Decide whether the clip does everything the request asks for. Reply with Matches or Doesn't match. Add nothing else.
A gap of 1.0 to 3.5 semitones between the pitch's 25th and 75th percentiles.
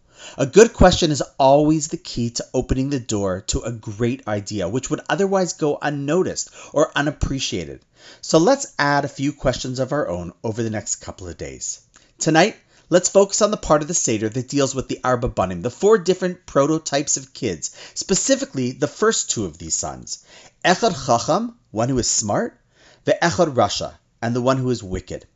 Doesn't match